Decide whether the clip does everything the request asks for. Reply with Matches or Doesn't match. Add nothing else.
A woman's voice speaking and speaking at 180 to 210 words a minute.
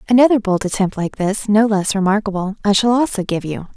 Matches